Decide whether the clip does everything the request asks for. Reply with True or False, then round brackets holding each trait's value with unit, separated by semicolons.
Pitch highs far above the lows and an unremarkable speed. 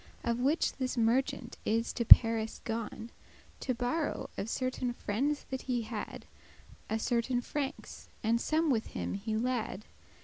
False (2.6 semitones; 160 wpm)